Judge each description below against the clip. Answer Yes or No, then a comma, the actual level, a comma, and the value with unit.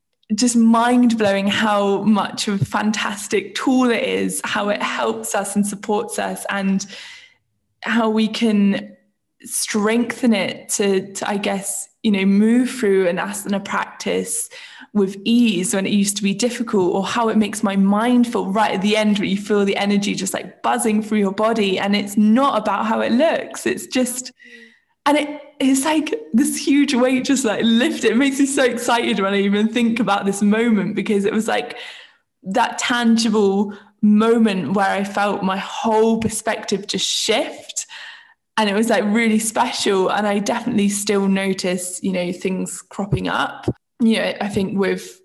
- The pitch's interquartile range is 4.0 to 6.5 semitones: No, average, 3.3 semitones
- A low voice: No, high, 215 Hz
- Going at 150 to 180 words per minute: Yes, average, 175 wpm